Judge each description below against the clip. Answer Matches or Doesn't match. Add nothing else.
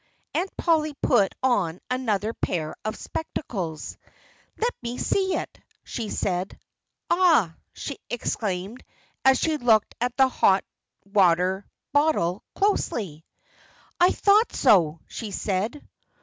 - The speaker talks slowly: Matches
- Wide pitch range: Matches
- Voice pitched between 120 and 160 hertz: Doesn't match